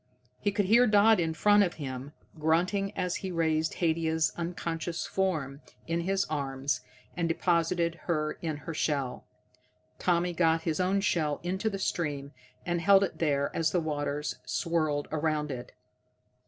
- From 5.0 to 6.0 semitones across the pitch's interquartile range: No, average, 3.0 semitones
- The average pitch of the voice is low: No, medium, 165 Hz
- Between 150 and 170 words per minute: Yes, average, 155 wpm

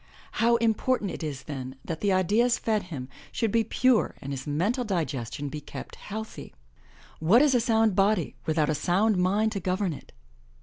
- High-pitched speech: Yes, high, 195 Hz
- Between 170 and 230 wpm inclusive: Yes, average, 180 wpm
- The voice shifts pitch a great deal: Yes, wide, 6.2 semitones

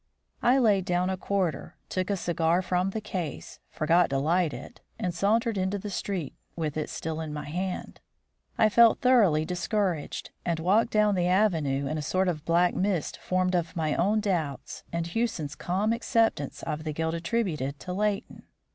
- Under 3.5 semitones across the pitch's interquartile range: No, average, 4.1 semitones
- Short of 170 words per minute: No, average, 180 wpm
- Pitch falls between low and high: Yes, medium, 180 Hz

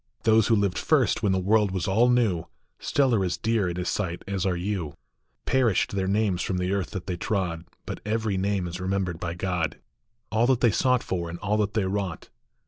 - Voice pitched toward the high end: No, very low, 95 Hz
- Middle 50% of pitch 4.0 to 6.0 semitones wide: No, average, 3.4 semitones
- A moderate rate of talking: No, fast, 220 wpm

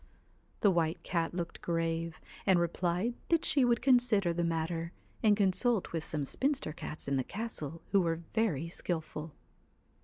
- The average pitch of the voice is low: No, medium, 170 Hz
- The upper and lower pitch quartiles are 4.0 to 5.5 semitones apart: Yes, average, 4.5 semitones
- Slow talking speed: No, average, 155 wpm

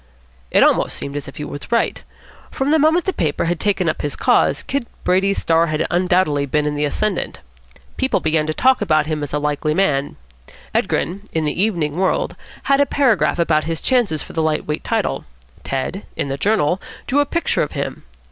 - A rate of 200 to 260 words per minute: Yes, fast, 205 wpm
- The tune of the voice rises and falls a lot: Yes, wide, 5.8 semitones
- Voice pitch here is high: No, medium, 165 Hz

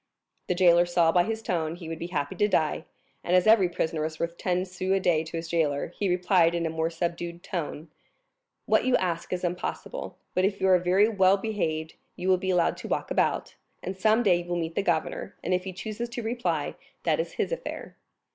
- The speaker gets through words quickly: Yes, fast, 225 wpm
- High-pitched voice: No, medium, 180 Hz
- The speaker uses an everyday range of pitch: No, narrow, 2.3 semitones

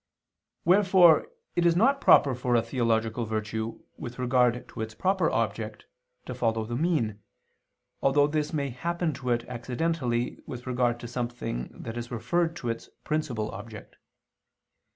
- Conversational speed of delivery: Yes, average, 150 wpm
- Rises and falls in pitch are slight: No, average, 5.2 semitones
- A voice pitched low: Yes, low, 125 Hz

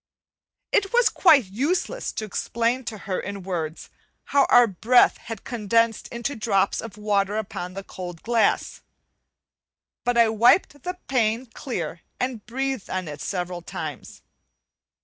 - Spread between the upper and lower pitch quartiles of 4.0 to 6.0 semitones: Yes, average, 4.5 semitones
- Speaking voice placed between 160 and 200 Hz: No, high, 225 Hz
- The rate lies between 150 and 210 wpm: No, average, 140 wpm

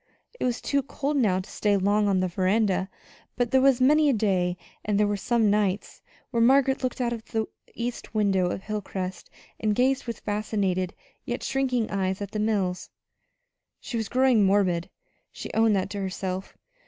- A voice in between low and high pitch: No, high, 210 Hz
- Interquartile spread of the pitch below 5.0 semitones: Yes, average, 4.1 semitones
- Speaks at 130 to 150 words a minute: No, average, 180 wpm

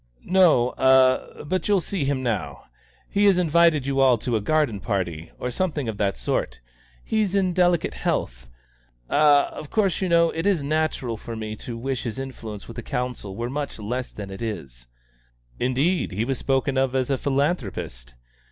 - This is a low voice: Yes, low, 130 Hz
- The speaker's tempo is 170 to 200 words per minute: Yes, average, 180 wpm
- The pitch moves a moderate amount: No, wide, 6.0 semitones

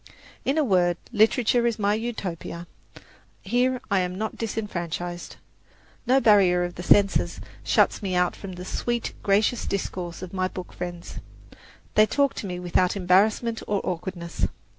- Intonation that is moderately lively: Yes, average, 3.7 semitones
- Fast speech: No, average, 150 wpm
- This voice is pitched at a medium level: No, high, 195 Hz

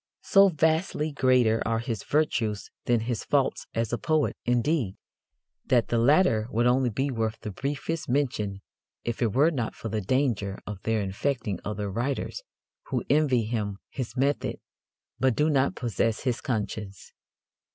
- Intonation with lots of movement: No, average, 4.4 semitones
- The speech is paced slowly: No, average, 155 wpm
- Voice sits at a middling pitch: No, low, 120 Hz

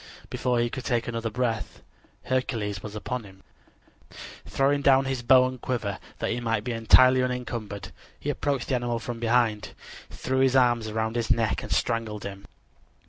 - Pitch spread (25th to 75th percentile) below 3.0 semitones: Yes, narrow, 2.4 semitones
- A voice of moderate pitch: No, low, 120 Hz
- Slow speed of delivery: No, average, 170 wpm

